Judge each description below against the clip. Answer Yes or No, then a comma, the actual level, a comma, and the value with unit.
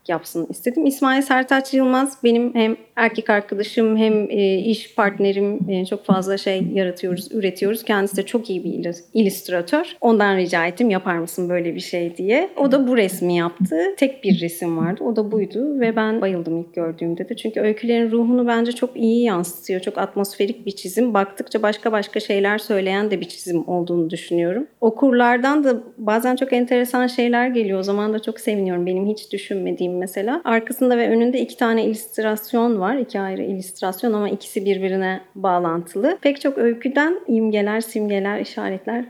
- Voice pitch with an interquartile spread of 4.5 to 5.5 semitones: No, average, 3.9 semitones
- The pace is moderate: No, fast, 165 wpm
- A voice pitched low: No, high, 210 Hz